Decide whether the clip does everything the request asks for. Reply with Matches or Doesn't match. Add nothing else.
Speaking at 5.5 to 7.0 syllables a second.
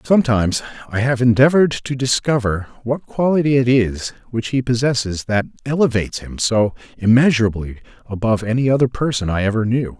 Matches